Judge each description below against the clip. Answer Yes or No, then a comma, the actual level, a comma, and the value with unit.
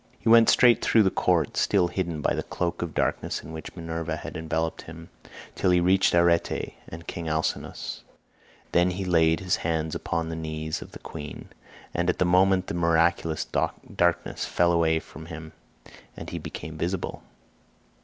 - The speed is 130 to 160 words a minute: No, average, 175 wpm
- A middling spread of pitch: No, narrow, 1.7 semitones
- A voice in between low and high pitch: No, very low, 85 Hz